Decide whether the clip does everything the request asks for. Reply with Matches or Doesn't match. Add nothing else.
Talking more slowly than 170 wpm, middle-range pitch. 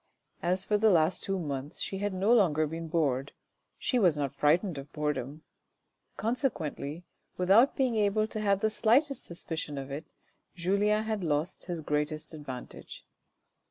Matches